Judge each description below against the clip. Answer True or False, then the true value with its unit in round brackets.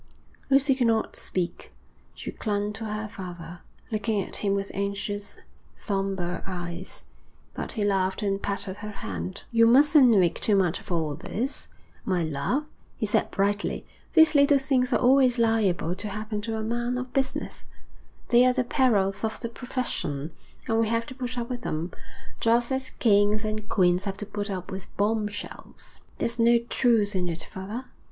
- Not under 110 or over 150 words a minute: False (175 wpm)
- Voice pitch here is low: False (210 Hz)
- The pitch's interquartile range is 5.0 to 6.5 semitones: False (3.7 semitones)